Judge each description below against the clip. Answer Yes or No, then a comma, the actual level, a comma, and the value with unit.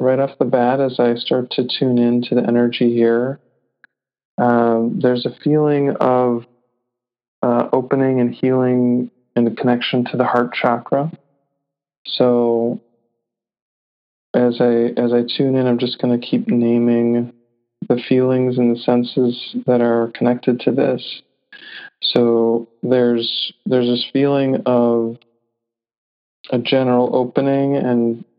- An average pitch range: No, narrow, 1.2 semitones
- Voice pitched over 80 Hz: Yes, low, 120 Hz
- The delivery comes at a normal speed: No, slow, 130 wpm